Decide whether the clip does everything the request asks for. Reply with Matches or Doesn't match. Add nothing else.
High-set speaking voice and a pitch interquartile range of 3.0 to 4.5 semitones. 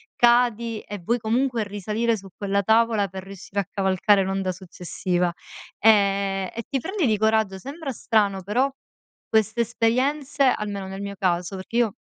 Matches